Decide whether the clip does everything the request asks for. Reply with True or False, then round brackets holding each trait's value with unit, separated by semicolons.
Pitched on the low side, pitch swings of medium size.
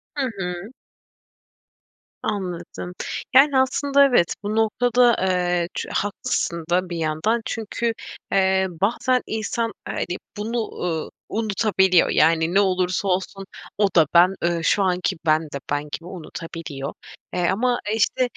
False (190 Hz; 4.5 semitones)